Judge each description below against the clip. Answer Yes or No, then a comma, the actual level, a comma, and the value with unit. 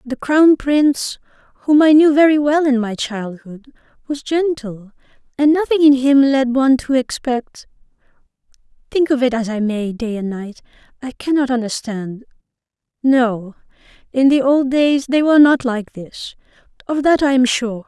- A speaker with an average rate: Yes, average, 160 wpm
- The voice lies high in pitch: Yes, very high, 260 Hz